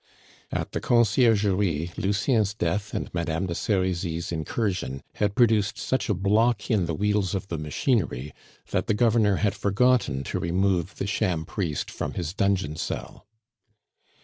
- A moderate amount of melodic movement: Yes, average, 3.8 semitones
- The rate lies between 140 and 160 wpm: Yes, average, 145 wpm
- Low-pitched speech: Yes, low, 100 Hz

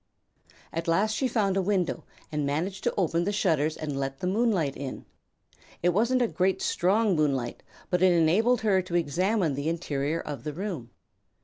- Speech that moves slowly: No, average, 180 wpm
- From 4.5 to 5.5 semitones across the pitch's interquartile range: Yes, average, 4.8 semitones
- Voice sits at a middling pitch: Yes, medium, 175 Hz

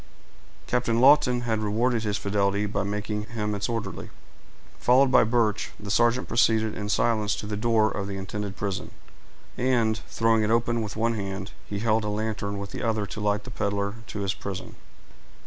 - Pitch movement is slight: Yes, narrow, 2.2 semitones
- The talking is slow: No, average, 180 wpm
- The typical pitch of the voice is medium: No, low, 105 Hz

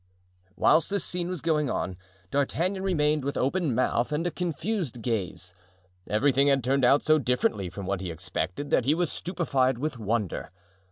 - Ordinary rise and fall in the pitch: No, wide, 5.9 semitones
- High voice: No, medium, 140 Hz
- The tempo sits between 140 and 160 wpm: No, average, 170 wpm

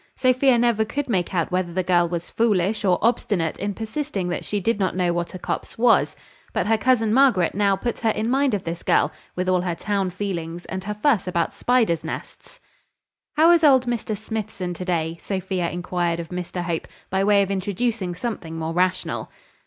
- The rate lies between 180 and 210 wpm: Yes, average, 200 wpm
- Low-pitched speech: No, high, 195 Hz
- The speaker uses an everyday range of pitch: Yes, average, 4.2 semitones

